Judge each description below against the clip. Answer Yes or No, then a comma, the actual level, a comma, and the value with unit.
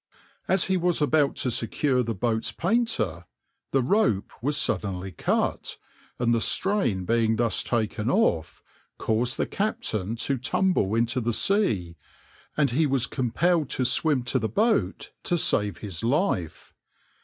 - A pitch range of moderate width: No, wide, 6.8 semitones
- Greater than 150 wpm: No, average, 145 wpm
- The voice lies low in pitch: Yes, low, 125 Hz